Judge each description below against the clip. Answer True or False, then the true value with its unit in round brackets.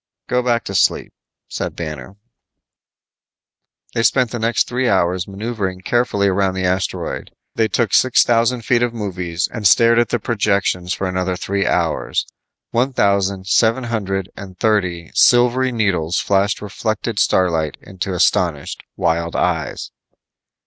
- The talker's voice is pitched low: True (100 Hz)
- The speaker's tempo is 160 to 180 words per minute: False (140 wpm)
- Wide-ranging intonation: False (4.1 semitones)